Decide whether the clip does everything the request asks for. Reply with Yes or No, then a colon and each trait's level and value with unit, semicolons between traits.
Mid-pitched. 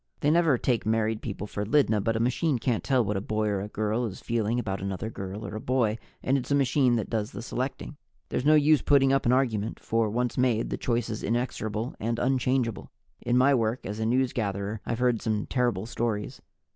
No: low, 115 Hz